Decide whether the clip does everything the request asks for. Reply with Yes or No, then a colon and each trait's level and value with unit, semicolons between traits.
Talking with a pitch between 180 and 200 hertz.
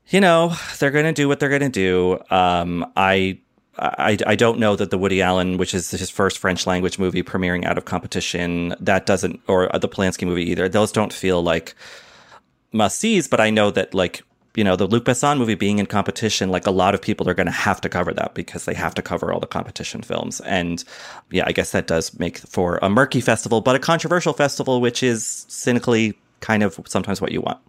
No: low, 105 Hz